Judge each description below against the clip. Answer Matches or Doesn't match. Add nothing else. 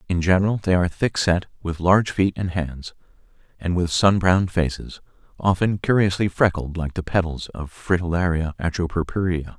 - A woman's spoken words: Doesn't match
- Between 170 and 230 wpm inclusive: Doesn't match